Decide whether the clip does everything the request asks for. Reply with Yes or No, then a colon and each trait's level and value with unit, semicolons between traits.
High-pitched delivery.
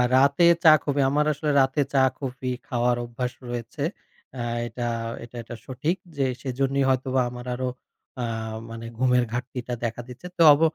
No: low, 130 Hz